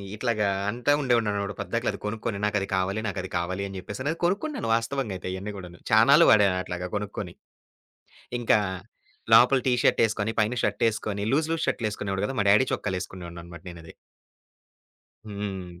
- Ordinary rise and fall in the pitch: Yes, average, 3.5 semitones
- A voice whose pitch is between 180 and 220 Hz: No, low, 105 Hz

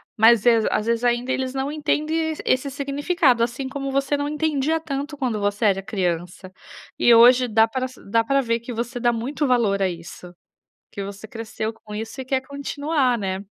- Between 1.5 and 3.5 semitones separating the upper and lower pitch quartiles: No, average, 4.1 semitones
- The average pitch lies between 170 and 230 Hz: No, high, 245 Hz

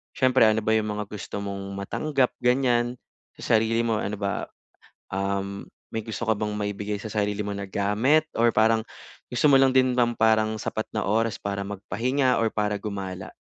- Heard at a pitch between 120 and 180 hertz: No, low, 110 Hz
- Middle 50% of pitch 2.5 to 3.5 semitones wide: Yes, average, 2.9 semitones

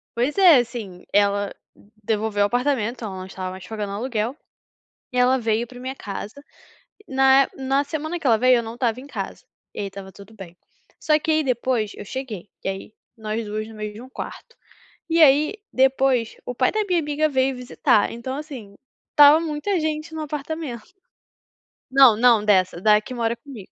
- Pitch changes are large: No, average, 4.9 semitones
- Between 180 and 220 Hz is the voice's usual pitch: No, high, 245 Hz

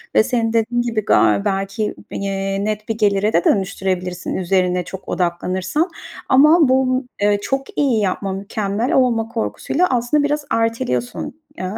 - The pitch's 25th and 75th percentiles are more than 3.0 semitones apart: Yes, average, 4.3 semitones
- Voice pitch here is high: Yes, high, 215 Hz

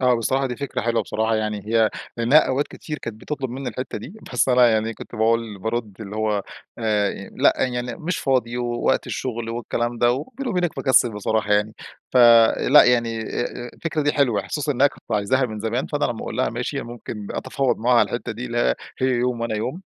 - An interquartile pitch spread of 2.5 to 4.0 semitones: Yes, average, 2.8 semitones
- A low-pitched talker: Yes, low, 120 Hz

